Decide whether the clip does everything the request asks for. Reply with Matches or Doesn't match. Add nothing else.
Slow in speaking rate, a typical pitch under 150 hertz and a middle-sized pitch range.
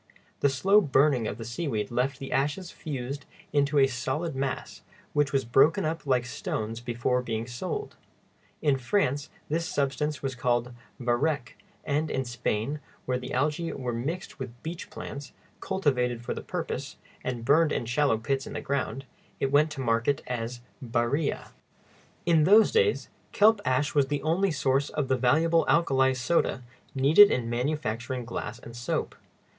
Doesn't match